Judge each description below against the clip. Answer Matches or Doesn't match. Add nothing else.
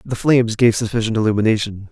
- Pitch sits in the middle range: Doesn't match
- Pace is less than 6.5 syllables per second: Doesn't match